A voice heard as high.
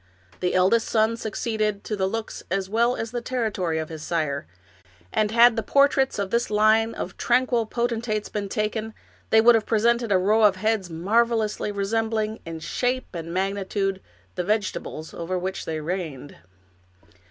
Yes: high, 215 Hz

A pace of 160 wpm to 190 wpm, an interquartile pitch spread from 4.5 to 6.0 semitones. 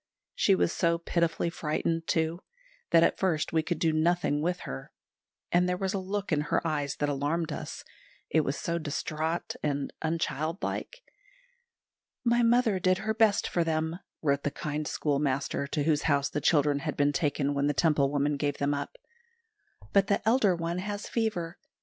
No: average, 175 wpm; average, 3.6 semitones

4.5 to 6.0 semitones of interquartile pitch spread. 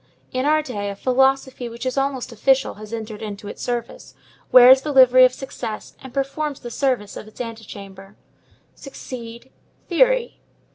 No: average, 3.4 semitones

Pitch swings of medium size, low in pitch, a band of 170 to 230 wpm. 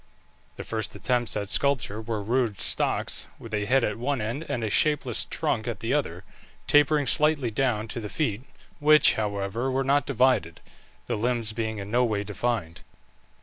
Yes: average, 4.1 semitones; low, 115 Hz; average, 175 wpm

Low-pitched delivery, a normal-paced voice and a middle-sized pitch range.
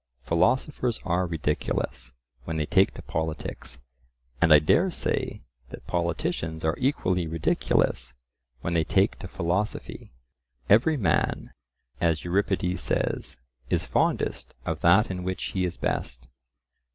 No: very low, 85 Hz; slow, 125 wpm; average, 3.2 semitones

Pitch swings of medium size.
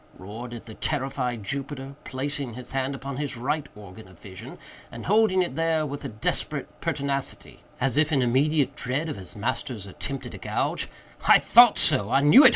Yes: average, 3.6 semitones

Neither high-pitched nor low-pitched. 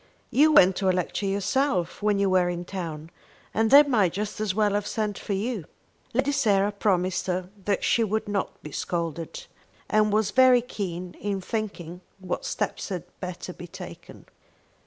No: high, 200 Hz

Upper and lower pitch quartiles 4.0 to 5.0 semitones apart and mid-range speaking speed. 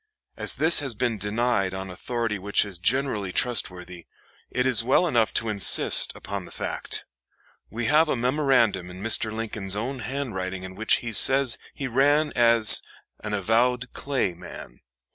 Yes: average, 4.4 semitones; average, 160 wpm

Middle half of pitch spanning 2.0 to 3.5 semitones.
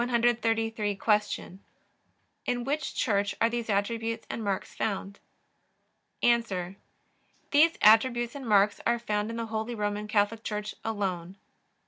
Yes: narrow, 2.4 semitones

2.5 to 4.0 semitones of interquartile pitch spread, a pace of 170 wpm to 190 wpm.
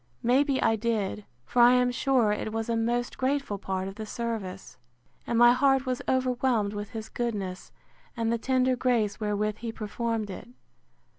Yes: average, 3.0 semitones; average, 175 wpm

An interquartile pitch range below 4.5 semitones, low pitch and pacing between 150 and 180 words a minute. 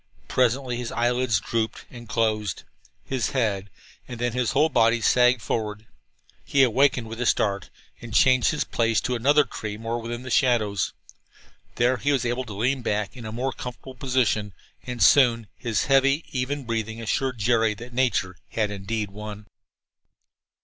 Yes: average, 2.7 semitones; low, 120 Hz; average, 165 wpm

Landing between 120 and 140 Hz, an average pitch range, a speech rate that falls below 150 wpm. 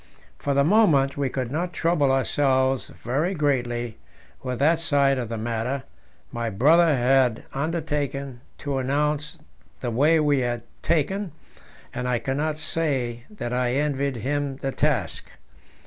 Yes: low, 135 Hz; average, 3.2 semitones; average, 140 wpm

